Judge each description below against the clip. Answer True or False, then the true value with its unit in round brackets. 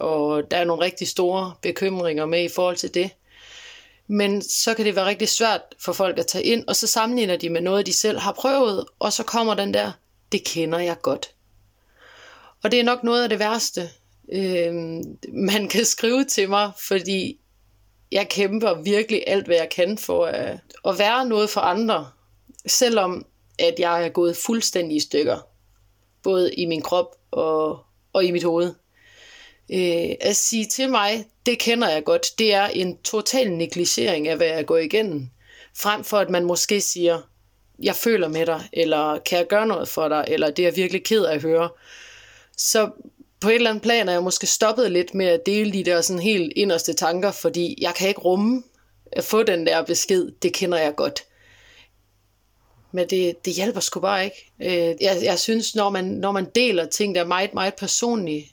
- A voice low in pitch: False (185 Hz)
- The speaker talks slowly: False (190 wpm)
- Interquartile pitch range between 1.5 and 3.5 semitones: False (4.2 semitones)